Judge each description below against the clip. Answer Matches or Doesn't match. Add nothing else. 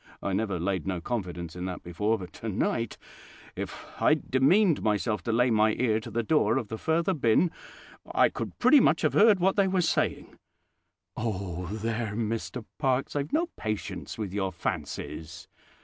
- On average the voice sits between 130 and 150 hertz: Doesn't match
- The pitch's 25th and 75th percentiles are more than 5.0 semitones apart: Matches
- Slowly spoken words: Doesn't match